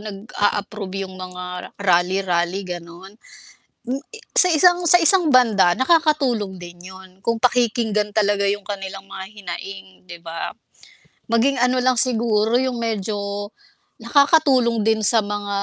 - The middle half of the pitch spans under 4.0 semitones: No, average, 4.5 semitones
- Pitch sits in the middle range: No, high, 205 Hz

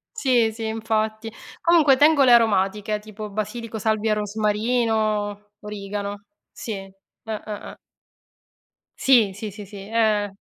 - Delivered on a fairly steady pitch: Yes, narrow, 1.7 semitones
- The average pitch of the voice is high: Yes, high, 215 Hz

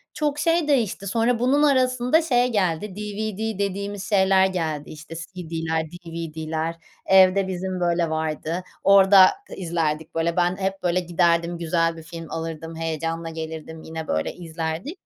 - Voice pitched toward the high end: No, medium, 175 Hz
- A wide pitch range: No, average, 3.5 semitones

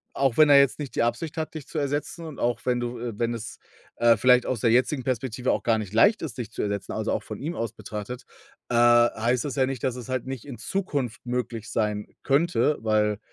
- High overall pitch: No, low, 125 Hz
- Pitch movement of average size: Yes, average, 3.3 semitones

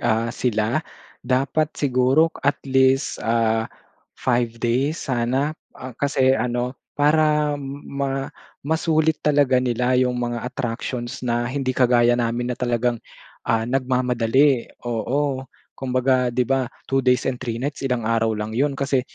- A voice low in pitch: Yes, low, 125 Hz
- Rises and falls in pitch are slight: Yes, narrow, 2.3 semitones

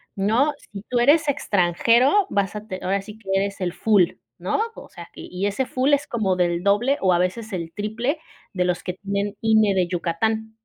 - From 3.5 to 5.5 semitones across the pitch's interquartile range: Yes, average, 4.0 semitones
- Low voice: No, high, 205 Hz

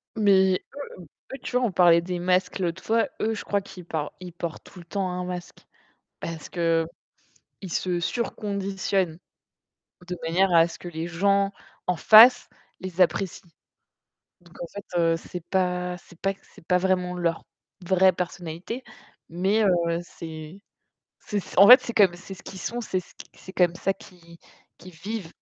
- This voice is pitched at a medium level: Yes, medium, 180 Hz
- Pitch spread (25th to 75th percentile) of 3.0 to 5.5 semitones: No, narrow, 2.4 semitones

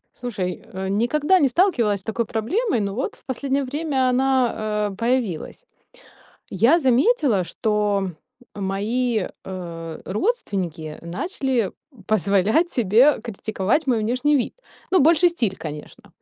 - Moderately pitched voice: No, high, 230 Hz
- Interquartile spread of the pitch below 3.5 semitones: No, wide, 5.5 semitones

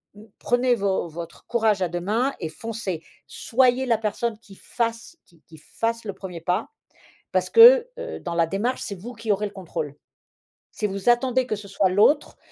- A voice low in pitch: No, high, 210 Hz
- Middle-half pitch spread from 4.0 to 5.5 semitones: Yes, average, 4.3 semitones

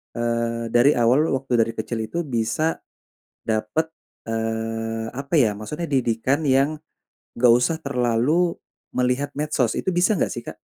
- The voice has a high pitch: No, low, 125 Hz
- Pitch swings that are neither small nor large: Yes, average, 4.1 semitones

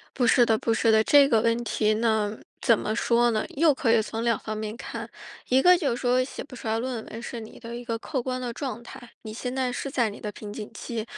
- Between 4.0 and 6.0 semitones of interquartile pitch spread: No, narrow, 2.4 semitones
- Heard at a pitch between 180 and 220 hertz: No, high, 235 Hz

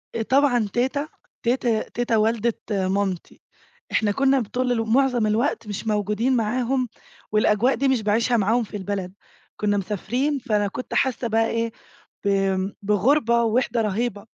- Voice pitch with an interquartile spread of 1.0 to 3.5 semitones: Yes, average, 3.1 semitones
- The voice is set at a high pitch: Yes, high, 230 Hz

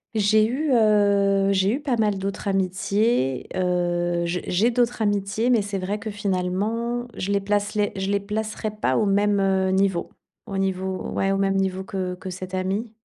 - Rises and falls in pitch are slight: Yes, narrow, 2.0 semitones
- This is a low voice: No, high, 200 Hz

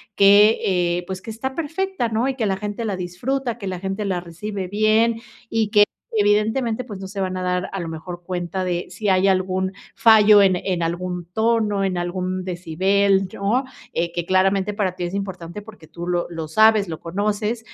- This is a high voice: Yes, high, 195 Hz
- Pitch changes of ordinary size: Yes, average, 3.1 semitones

